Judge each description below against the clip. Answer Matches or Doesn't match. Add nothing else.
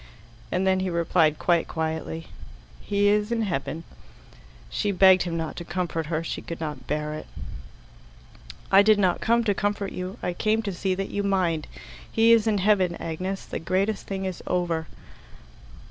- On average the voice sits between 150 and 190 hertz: Matches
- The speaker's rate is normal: Matches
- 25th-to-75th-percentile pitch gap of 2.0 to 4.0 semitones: Matches